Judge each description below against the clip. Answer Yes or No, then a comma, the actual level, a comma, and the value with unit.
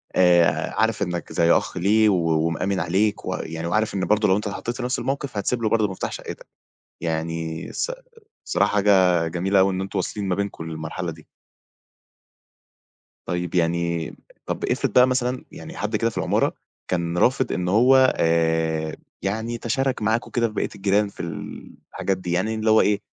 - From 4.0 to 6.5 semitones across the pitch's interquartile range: Yes, average, 4.4 semitones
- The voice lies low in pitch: Yes, very low, 95 Hz